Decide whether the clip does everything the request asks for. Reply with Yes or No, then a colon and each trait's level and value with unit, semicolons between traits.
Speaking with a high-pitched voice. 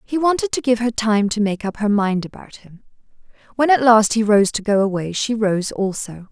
Yes: high, 220 Hz